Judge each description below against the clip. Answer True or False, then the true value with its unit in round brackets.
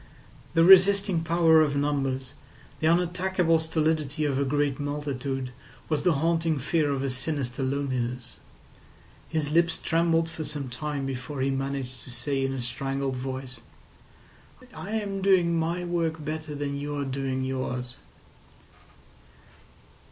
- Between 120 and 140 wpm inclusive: True (135 wpm)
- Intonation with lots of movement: False (3.5 semitones)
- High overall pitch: False (145 Hz)